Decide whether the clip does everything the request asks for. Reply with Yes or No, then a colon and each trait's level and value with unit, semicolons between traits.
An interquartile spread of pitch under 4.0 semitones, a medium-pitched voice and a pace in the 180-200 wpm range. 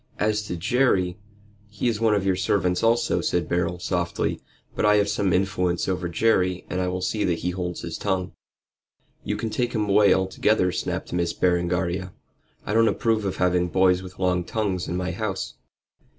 No: average, 2.8 semitones; very low, 95 Hz; average, 190 wpm